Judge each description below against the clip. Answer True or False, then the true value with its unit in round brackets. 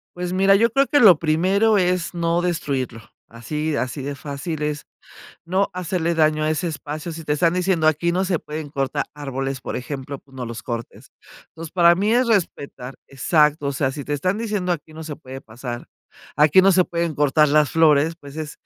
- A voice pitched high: False (155 Hz)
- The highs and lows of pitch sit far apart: False (3.9 semitones)